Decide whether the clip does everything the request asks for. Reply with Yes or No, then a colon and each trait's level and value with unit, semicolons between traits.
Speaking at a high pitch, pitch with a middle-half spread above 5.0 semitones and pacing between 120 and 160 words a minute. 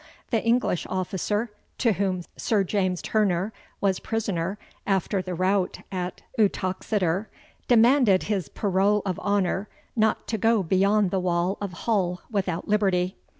No: high, 195 Hz; narrow, 2.5 semitones; slow, 135 wpm